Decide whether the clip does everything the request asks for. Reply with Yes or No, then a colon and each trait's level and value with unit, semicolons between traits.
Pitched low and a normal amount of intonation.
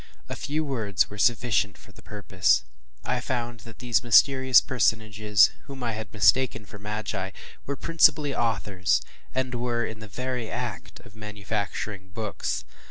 Yes: low, 110 Hz; average, 3.4 semitones